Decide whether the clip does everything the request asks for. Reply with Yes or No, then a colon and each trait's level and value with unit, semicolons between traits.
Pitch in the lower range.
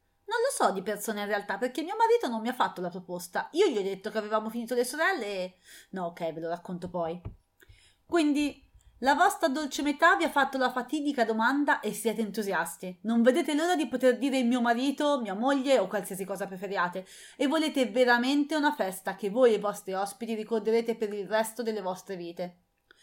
No: high, 230 Hz